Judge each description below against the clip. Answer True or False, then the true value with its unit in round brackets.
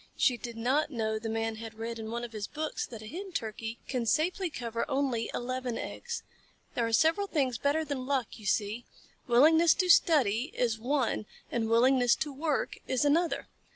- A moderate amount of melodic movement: True (4.6 semitones)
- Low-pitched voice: False (245 Hz)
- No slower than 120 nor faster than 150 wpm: False (190 wpm)